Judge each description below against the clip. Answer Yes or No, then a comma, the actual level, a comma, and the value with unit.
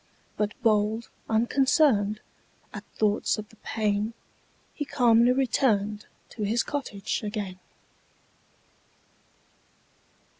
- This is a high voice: Yes, high, 220 Hz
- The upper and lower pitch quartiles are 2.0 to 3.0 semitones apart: Yes, narrow, 2.6 semitones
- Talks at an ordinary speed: No, slow, 85 wpm